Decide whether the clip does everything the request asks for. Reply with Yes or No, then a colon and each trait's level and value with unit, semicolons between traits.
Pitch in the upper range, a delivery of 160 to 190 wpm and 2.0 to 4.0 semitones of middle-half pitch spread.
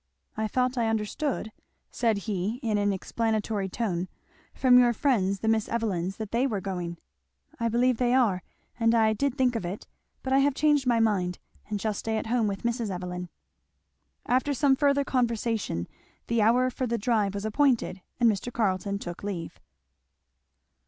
Yes: high, 225 Hz; average, 170 wpm; average, 3.7 semitones